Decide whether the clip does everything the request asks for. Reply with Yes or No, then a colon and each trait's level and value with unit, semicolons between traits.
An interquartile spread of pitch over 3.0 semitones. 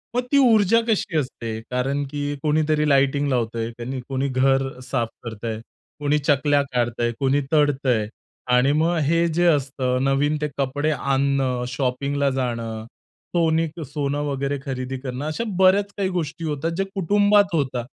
Yes: average, 3.4 semitones